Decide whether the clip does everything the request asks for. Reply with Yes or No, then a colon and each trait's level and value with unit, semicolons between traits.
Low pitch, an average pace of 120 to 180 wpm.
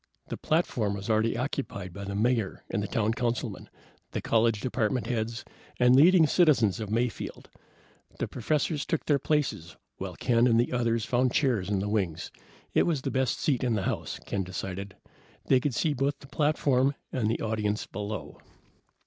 Yes: low, 115 Hz; average, 175 wpm